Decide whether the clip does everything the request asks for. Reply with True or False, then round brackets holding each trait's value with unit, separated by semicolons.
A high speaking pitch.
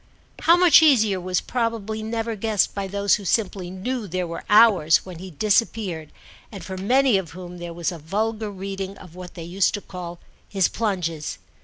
True (195 Hz)